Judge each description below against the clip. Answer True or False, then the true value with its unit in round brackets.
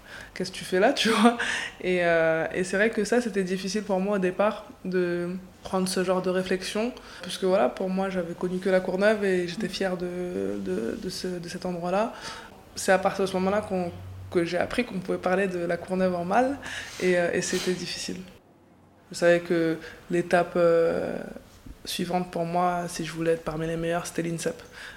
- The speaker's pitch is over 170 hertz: True (185 Hz)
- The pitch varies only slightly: True (1.8 semitones)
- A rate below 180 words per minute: False (205 wpm)